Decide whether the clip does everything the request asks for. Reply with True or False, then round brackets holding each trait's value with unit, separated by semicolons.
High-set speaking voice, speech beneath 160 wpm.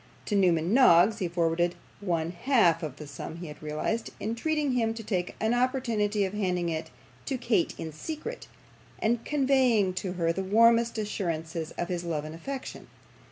False (195 Hz; 170 wpm)